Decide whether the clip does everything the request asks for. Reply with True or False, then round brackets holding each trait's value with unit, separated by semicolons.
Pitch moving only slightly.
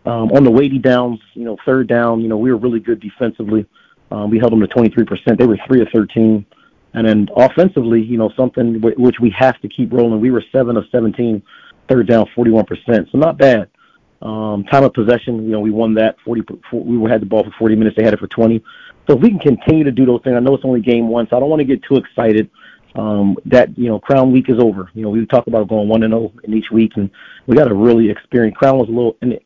True (2.2 semitones)